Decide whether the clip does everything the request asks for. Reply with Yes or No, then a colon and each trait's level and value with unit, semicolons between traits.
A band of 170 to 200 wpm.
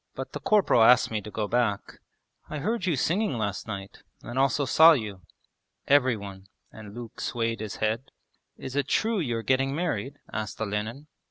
Yes: average, 180 wpm